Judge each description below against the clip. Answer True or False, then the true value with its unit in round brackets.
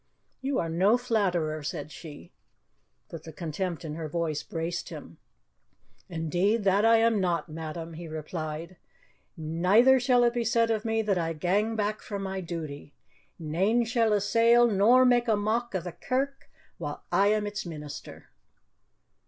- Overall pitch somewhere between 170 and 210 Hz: True (190 Hz)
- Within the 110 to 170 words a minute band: True (160 wpm)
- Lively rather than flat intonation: True (5.7 semitones)